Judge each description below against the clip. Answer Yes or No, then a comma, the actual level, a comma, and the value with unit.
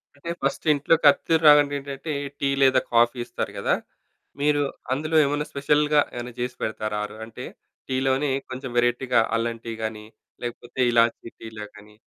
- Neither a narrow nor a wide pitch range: Yes, average, 3.7 semitones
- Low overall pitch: Yes, low, 130 Hz